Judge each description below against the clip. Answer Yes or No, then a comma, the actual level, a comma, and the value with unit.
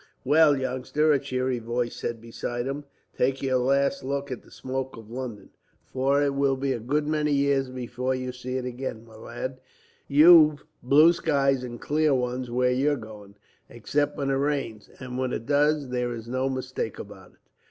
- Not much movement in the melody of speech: Yes, narrow, 2.2 semitones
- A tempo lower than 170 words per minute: No, average, 185 wpm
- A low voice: Yes, low, 130 Hz